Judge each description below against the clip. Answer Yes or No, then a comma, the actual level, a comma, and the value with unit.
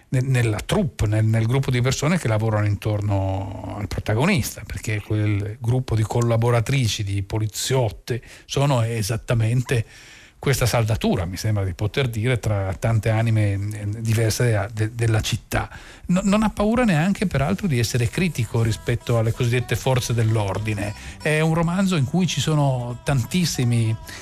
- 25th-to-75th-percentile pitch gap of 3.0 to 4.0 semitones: Yes, average, 3.5 semitones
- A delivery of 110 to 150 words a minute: Yes, average, 140 wpm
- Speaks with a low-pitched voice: Yes, low, 115 Hz